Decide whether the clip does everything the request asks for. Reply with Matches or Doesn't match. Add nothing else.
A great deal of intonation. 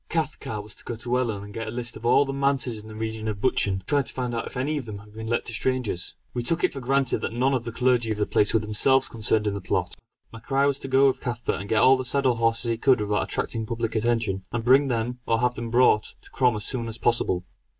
Doesn't match